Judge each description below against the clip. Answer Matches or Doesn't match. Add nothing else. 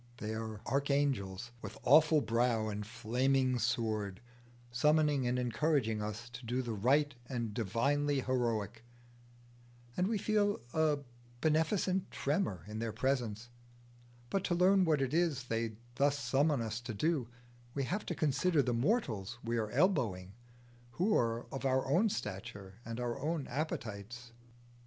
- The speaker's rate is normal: Matches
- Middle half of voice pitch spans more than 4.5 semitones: Matches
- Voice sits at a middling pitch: Doesn't match